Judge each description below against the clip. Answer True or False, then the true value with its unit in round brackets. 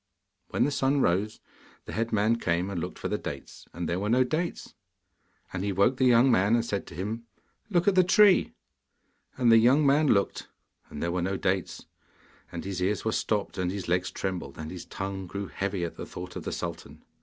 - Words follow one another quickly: True (215 wpm)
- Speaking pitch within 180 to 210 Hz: False (100 Hz)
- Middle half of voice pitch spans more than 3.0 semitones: True (5.0 semitones)